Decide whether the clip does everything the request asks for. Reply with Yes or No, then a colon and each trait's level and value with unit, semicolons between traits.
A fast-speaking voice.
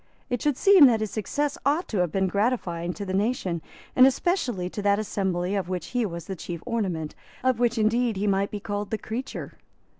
Yes: fast, 210 wpm